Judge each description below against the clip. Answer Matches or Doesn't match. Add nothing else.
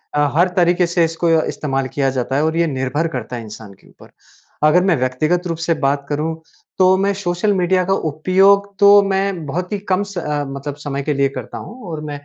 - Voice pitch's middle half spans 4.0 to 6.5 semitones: Matches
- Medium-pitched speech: Matches